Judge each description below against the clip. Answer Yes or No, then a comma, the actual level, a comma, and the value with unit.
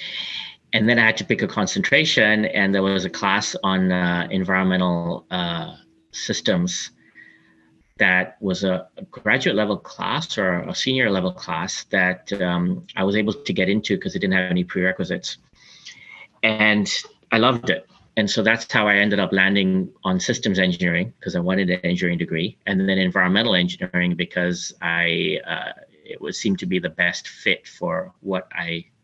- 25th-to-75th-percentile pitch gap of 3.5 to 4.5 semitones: No, average, 2.9 semitones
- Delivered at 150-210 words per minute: Yes, average, 165 wpm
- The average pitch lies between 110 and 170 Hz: No, very low, 95 Hz